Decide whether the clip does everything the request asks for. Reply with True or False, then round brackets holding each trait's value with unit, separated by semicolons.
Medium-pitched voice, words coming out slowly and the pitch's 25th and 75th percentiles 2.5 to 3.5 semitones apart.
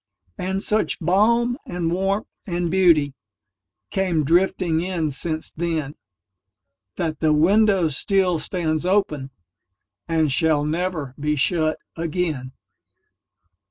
False (160 Hz; 90 wpm; 5.0 semitones)